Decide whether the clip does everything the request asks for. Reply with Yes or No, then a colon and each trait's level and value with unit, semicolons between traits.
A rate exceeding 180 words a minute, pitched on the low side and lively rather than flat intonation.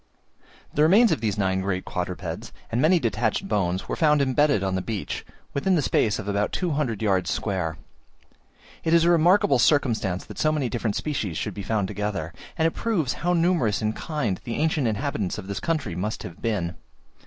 Yes: average, 190 wpm; low, 110 Hz; wide, 7.9 semitones